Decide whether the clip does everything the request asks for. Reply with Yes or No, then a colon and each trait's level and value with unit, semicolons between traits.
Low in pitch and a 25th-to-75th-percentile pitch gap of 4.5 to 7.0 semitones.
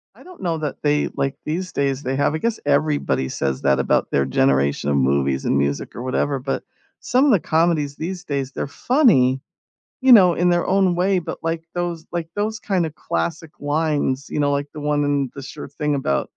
No: medium, 150 Hz; average, 5.0 semitones